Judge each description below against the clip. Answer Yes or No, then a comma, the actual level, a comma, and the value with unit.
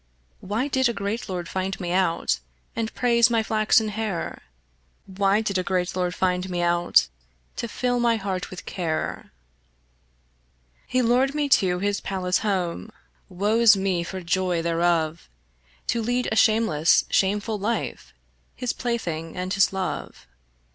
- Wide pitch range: No, average, 4.0 semitones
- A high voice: Yes, high, 195 Hz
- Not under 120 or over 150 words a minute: Yes, average, 145 wpm